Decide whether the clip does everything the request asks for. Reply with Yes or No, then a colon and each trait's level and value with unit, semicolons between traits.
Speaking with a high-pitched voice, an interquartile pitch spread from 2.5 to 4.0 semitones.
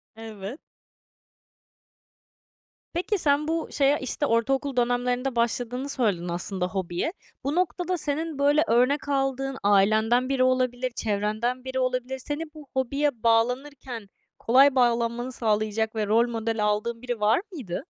Yes: very high, 250 Hz; average, 3.7 semitones